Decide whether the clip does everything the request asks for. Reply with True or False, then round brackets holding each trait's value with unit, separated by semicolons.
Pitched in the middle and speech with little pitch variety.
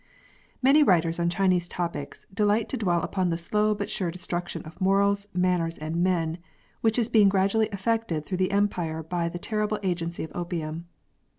False (180 Hz; 3.2 semitones)